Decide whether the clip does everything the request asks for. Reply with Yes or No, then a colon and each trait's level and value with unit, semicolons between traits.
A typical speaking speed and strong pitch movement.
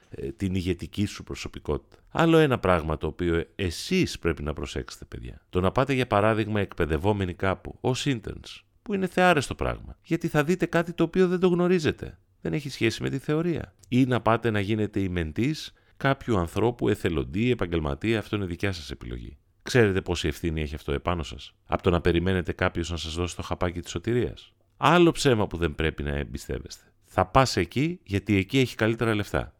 No: fast, 185 wpm; wide, 6.9 semitones